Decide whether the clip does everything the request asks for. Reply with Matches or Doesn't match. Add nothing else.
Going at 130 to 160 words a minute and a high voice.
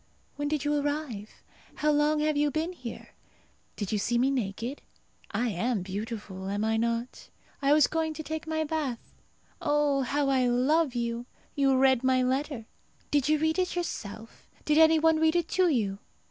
Doesn't match